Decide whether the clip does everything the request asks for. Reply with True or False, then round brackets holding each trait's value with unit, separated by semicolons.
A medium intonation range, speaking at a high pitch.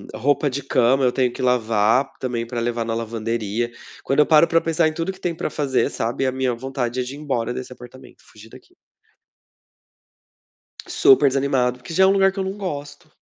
False (3.7 semitones; 130 Hz)